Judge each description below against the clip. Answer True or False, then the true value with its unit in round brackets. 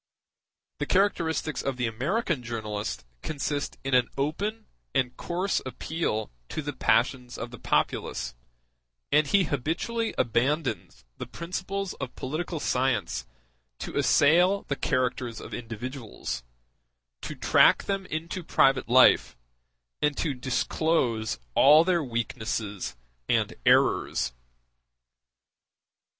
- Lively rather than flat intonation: True (5.8 semitones)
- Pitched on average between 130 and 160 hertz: True (135 Hz)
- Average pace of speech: False (110 wpm)